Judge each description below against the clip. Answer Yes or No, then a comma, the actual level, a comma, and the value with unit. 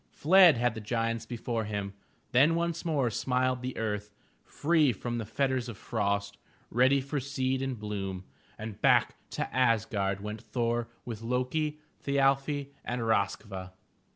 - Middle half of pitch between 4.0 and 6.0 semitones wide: Yes, average, 4.3 semitones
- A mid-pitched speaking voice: No, low, 120 Hz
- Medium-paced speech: Yes, average, 155 wpm